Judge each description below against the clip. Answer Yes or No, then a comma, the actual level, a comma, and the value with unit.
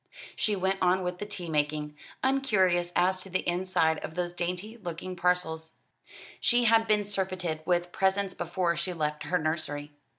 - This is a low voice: No, medium, 180 Hz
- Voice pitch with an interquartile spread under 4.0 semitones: Yes, narrow, 2.6 semitones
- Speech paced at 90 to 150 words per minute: No, average, 165 wpm